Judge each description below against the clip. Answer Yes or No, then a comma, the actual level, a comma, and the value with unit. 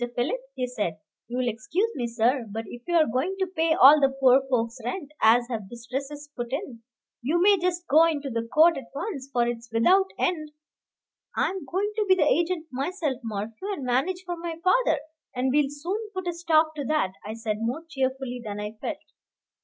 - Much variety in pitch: Yes, wide, 6.1 semitones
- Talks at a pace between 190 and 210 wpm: Yes, average, 200 wpm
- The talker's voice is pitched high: Yes, very high, 275 Hz